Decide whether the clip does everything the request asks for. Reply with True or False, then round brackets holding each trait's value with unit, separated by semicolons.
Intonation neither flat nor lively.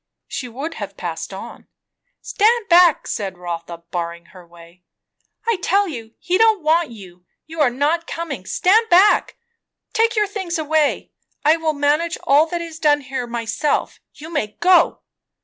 False (7.3 semitones)